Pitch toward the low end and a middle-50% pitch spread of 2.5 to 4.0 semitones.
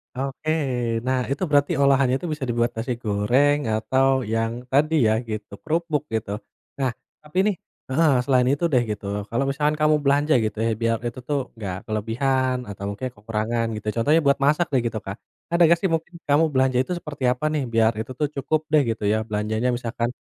No: low, 130 Hz; average, 4.6 semitones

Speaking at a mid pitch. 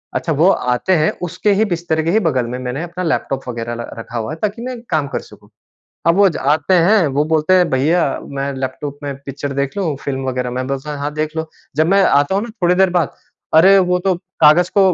Yes: medium, 155 Hz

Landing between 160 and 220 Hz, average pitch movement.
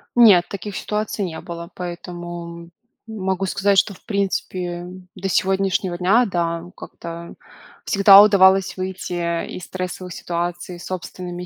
No: medium, 185 Hz; narrow, 2.1 semitones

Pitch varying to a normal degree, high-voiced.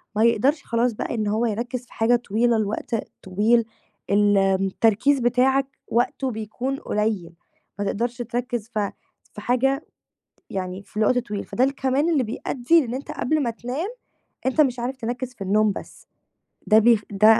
Yes: average, 3.3 semitones; high, 235 Hz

